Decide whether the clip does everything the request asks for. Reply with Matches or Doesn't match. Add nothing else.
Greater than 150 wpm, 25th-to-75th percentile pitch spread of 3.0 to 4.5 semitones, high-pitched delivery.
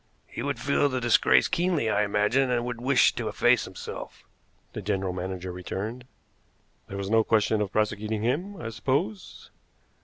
Doesn't match